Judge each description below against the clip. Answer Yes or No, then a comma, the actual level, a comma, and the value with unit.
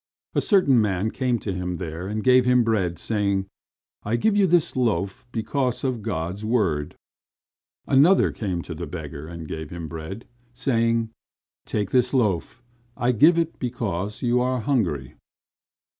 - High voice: No, low, 110 Hz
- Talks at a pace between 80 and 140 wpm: No, average, 155 wpm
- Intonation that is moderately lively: No, wide, 6.0 semitones